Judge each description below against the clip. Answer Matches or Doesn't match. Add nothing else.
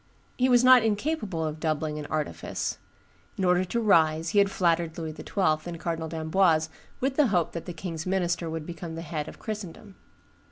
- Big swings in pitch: Doesn't match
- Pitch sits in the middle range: Matches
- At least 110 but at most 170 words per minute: Doesn't match